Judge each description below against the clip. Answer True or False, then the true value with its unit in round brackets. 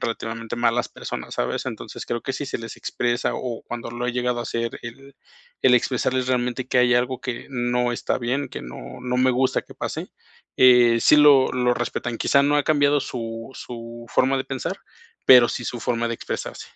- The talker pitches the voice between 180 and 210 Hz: False (125 Hz)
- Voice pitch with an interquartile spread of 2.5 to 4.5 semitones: False (1.6 semitones)